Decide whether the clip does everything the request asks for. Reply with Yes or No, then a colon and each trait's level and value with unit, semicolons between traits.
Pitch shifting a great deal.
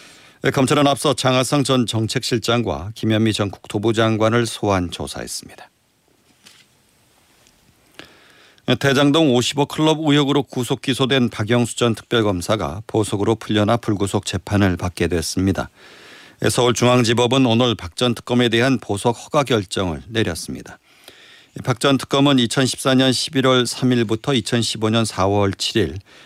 No: average, 3.7 semitones